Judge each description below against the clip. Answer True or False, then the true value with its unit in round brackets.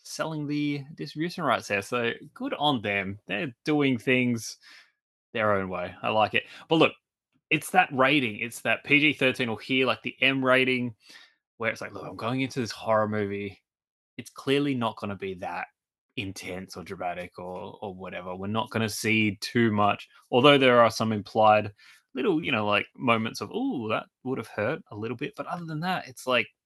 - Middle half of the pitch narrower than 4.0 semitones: False (4.5 semitones)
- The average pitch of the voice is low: True (115 Hz)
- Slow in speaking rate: False (195 wpm)